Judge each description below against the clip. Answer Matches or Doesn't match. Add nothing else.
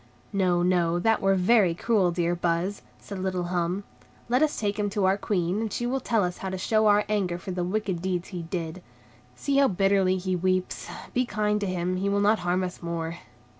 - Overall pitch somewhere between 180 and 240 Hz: Matches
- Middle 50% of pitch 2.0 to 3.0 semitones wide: Matches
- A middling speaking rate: Doesn't match